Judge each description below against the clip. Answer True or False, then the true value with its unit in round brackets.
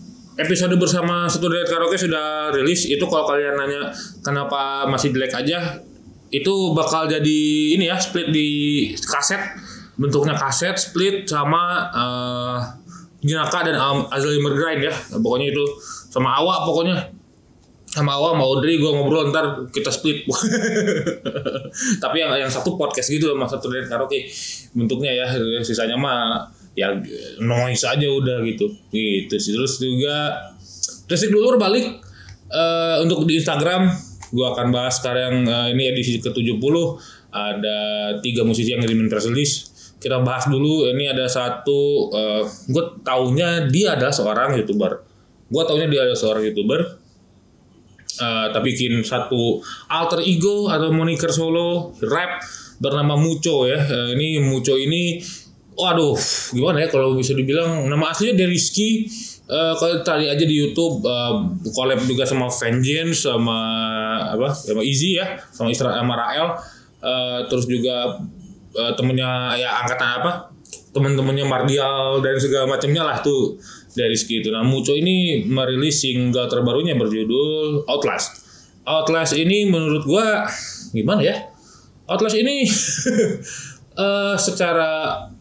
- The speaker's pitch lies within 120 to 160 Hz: True (140 Hz)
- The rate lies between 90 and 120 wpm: False (130 wpm)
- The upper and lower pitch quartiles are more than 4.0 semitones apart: True (5.2 semitones)